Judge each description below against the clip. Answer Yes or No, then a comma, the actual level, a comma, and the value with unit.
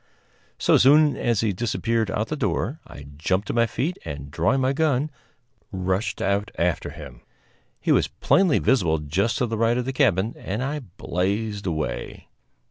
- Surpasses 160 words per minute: Yes, average, 180 wpm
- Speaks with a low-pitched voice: Yes, low, 110 Hz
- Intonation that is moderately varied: No, wide, 5.7 semitones